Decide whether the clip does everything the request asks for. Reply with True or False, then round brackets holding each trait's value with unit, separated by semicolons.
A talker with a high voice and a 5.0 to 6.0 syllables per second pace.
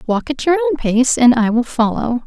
True (235 Hz; 5.1 syllables/s)